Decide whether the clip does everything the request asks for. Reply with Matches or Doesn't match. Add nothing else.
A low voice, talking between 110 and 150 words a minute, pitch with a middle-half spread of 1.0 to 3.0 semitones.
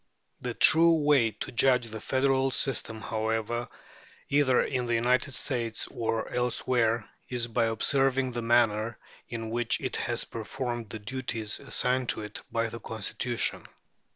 Matches